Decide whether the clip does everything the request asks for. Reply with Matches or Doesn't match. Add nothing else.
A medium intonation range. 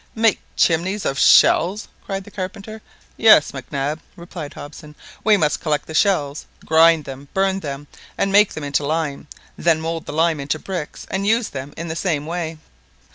Matches